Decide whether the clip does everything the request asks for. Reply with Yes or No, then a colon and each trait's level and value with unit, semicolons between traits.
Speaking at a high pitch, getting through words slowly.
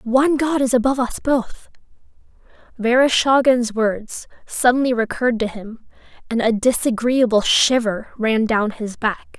Yes: high, 240 Hz; slow, 120 wpm